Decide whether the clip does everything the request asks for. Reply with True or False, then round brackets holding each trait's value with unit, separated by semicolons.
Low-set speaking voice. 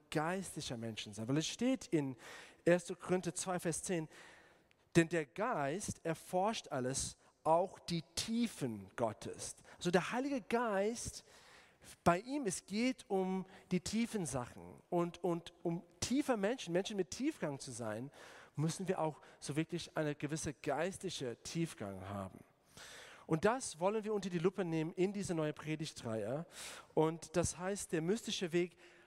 False (175 Hz)